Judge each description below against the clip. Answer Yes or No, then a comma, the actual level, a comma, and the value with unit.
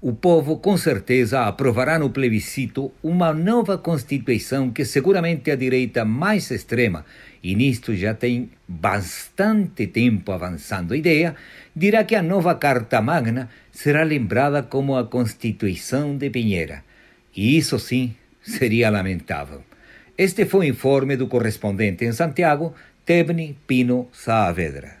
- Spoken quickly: No, average, 130 wpm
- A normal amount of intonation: No, wide, 6.2 semitones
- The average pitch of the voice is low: Yes, low, 130 Hz